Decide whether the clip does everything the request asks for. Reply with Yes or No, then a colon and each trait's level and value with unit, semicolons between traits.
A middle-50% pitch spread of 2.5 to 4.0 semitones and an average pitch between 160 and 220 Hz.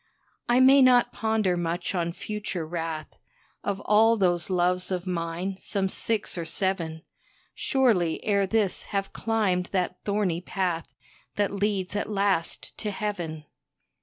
Yes: average, 3.2 semitones; high, 190 Hz